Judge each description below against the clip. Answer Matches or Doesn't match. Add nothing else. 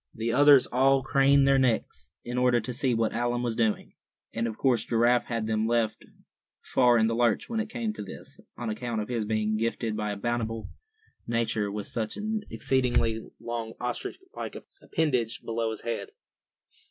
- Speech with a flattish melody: Matches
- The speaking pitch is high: Doesn't match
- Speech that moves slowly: Doesn't match